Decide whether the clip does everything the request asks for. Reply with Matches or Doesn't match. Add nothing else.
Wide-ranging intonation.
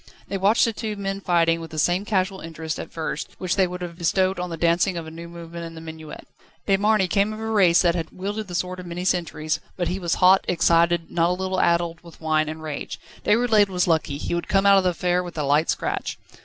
Doesn't match